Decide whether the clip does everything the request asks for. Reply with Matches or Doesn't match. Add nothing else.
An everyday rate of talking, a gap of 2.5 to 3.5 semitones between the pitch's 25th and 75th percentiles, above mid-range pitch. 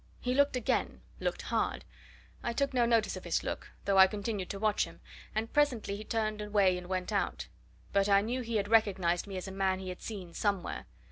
Doesn't match